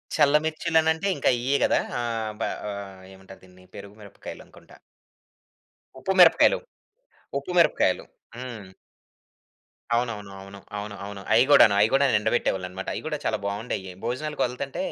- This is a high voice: No, low, 115 Hz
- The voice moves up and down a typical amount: No, wide, 5.9 semitones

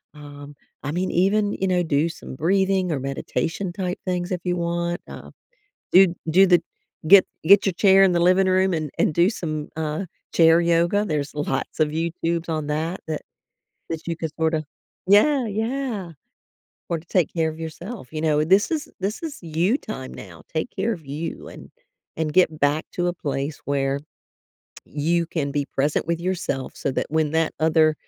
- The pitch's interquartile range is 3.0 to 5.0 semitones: Yes, average, 3.4 semitones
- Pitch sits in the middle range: Yes, medium, 170 Hz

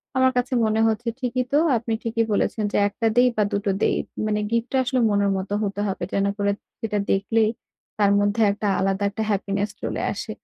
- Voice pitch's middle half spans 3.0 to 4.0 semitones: No, narrow, 2.4 semitones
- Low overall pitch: No, high, 210 Hz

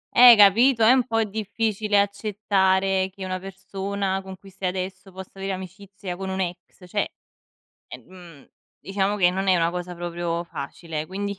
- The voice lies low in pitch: No, high, 190 Hz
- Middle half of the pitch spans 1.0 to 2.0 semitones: Yes, narrow, 1.7 semitones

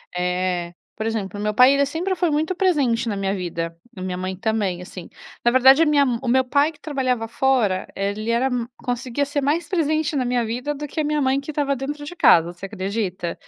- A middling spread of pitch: No, wide, 6.7 semitones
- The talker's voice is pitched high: Yes, high, 245 Hz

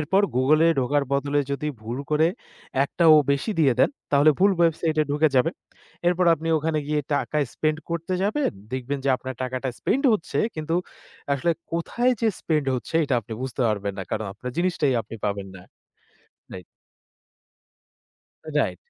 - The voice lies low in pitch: No, medium, 150 Hz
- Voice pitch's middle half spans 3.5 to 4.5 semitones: Yes, average, 4.0 semitones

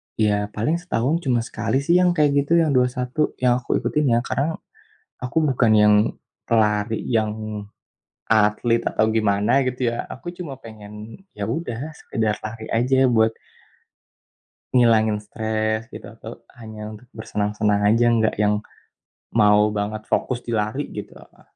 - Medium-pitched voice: No, low, 115 Hz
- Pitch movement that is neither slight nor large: Yes, average, 3.2 semitones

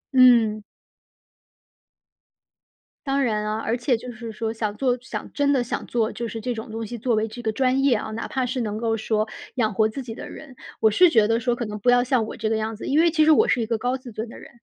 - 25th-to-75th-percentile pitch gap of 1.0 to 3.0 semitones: Yes, narrow, 2.6 semitones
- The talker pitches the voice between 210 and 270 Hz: Yes, high, 230 Hz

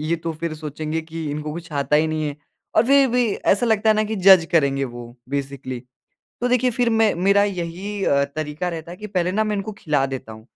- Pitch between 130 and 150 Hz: No, medium, 170 Hz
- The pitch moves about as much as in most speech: No, wide, 5.8 semitones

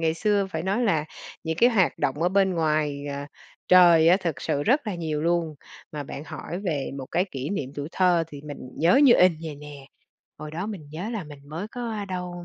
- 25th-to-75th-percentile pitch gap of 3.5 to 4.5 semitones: Yes, average, 4.0 semitones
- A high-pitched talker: No, medium, 165 Hz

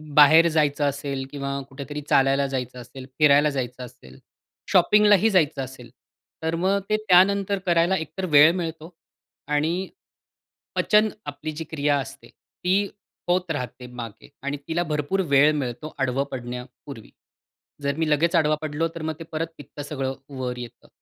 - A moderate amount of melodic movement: Yes, average, 3.6 semitones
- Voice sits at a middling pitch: Yes, medium, 150 Hz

